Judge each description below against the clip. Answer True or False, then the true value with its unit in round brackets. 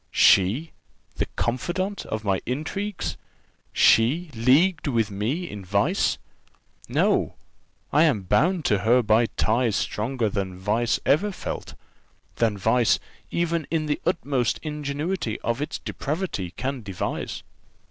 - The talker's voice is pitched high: False (125 Hz)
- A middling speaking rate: False (125 wpm)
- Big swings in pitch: True (6.8 semitones)